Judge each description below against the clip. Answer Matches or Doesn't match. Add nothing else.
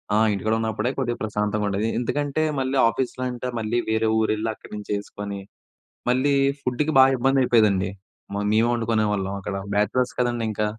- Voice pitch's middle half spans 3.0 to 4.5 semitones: Matches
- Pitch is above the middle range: Doesn't match